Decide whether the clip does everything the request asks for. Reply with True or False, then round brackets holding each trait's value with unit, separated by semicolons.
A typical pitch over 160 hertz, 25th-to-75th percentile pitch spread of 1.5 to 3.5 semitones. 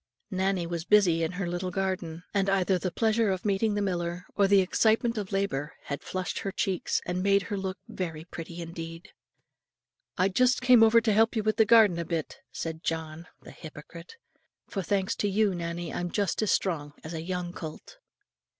True (185 Hz; 3.2 semitones)